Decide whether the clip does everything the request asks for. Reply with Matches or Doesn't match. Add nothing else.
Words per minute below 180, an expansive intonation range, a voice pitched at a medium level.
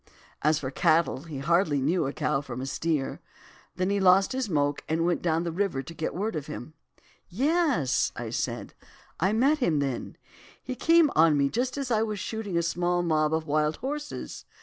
Doesn't match